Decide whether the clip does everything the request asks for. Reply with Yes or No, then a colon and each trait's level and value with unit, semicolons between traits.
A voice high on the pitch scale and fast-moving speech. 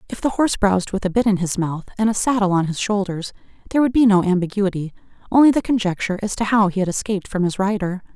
Yes: high, 200 Hz; fast, 235 wpm